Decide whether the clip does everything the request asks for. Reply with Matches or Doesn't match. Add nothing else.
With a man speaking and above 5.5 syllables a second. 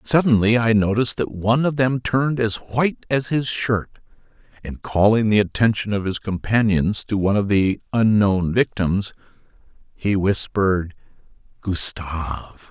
Doesn't match